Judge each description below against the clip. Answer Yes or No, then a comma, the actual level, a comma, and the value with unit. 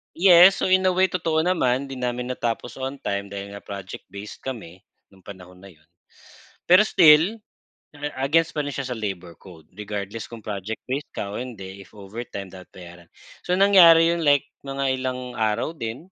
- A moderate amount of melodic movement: No, wide, 8.0 semitones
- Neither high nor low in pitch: No, low, 125 Hz